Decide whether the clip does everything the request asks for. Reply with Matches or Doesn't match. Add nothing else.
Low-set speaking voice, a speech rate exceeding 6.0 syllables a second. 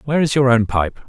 Matches